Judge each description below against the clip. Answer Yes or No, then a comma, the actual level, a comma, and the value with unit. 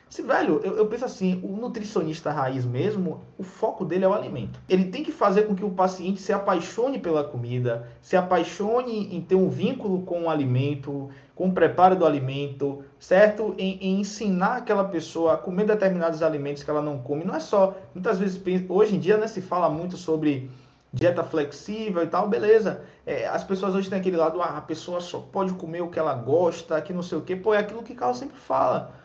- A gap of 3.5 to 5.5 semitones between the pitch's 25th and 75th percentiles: Yes, average, 4.4 semitones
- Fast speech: Yes, fast, 215 wpm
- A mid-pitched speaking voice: Yes, medium, 180 Hz